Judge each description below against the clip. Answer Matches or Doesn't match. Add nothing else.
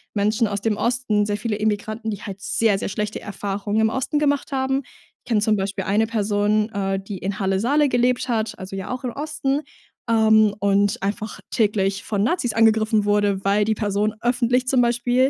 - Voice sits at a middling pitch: Doesn't match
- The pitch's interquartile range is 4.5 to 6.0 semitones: Doesn't match